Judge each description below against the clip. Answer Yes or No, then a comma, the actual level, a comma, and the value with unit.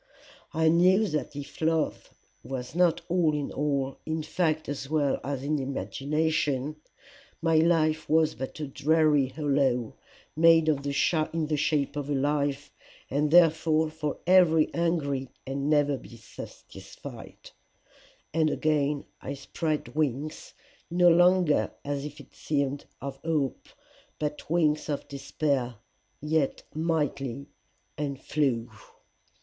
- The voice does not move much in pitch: Yes, narrow, 2.3 semitones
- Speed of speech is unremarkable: No, slow, 125 wpm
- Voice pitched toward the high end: No, medium, 150 Hz